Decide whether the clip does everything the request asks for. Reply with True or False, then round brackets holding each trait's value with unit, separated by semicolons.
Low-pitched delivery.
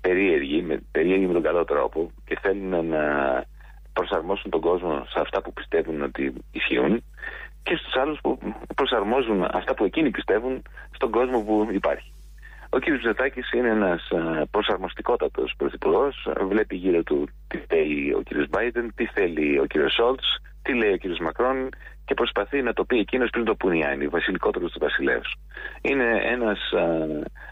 True (100 Hz)